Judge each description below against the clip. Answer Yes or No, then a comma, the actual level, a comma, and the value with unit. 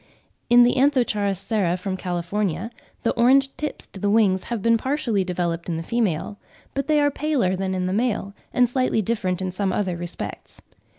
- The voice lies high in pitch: Yes, high, 205 Hz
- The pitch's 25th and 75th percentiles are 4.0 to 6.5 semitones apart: Yes, average, 4.8 semitones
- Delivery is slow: No, average, 185 wpm